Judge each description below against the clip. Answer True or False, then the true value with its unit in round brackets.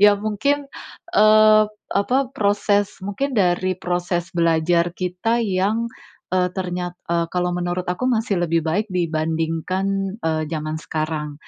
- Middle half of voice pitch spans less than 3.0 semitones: False (3.6 semitones)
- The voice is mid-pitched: True (180 Hz)